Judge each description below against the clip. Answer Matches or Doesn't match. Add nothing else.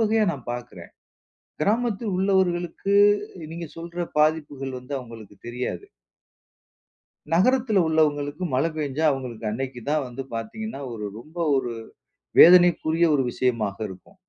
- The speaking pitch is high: Doesn't match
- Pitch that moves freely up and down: Matches